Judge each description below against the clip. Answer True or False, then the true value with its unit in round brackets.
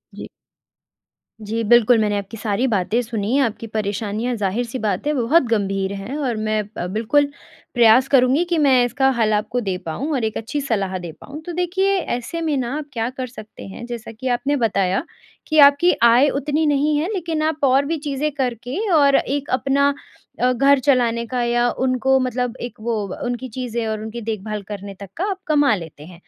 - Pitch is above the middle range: True (245 Hz)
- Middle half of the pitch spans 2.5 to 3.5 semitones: False (4.4 semitones)